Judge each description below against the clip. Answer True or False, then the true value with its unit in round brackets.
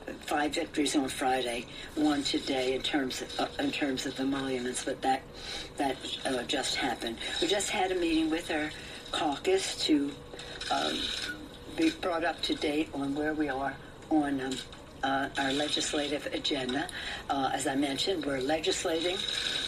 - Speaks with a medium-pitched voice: True (145 Hz)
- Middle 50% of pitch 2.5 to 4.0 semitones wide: True (2.9 semitones)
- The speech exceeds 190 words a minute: False (155 wpm)